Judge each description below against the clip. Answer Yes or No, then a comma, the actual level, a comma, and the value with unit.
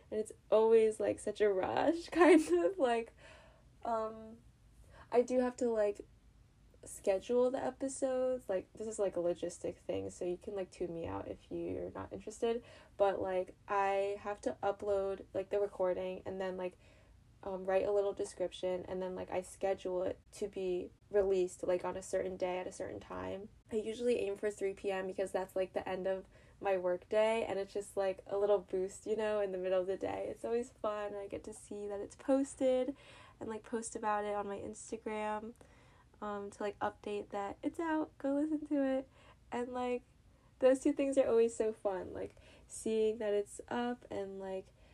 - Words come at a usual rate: Yes, average, 195 wpm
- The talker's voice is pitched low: No, high, 205 Hz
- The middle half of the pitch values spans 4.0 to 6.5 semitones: No, average, 3.4 semitones